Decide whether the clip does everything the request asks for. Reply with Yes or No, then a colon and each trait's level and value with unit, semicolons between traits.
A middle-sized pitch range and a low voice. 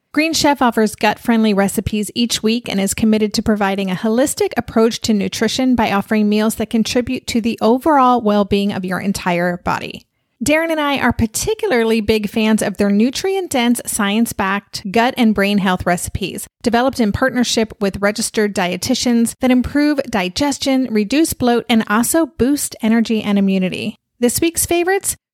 No: average, 3.6 semitones; high, 225 Hz